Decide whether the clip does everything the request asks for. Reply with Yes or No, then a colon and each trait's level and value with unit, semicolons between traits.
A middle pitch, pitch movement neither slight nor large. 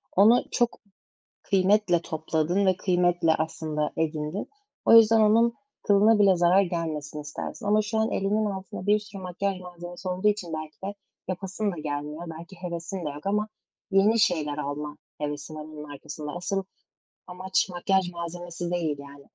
Yes: medium, 180 Hz; average, 4.1 semitones